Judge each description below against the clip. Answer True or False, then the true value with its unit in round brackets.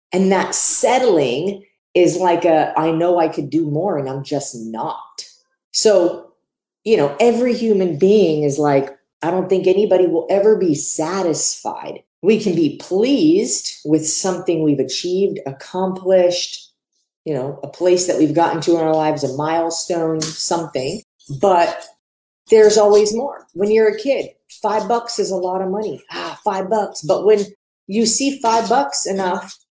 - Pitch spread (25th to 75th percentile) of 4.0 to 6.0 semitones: True (4.7 semitones)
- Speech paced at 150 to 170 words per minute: True (160 wpm)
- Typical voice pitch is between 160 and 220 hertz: True (185 Hz)